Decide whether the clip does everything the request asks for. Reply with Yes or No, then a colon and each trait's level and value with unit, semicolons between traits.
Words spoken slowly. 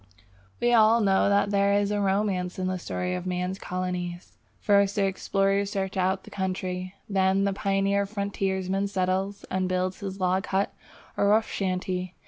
No: average, 165 wpm